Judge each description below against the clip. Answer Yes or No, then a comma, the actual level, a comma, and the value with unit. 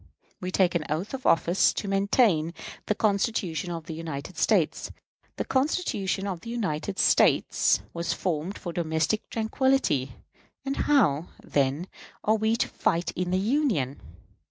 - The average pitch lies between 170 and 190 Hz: Yes, medium, 185 Hz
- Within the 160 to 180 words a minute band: No, average, 145 wpm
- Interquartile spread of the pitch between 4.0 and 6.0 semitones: Yes, average, 5.2 semitones